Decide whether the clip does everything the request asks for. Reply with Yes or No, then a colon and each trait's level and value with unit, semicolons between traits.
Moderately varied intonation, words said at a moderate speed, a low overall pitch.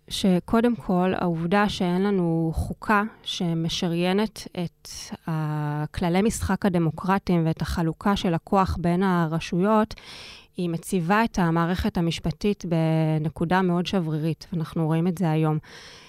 No: average, 3.0 semitones; average, 110 wpm; medium, 175 Hz